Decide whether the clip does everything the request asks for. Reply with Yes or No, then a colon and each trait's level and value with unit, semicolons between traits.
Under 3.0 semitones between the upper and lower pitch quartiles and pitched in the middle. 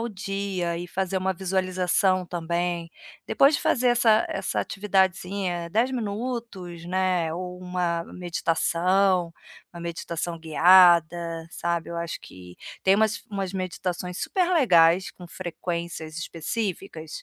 Yes: narrow, 2.4 semitones; medium, 180 Hz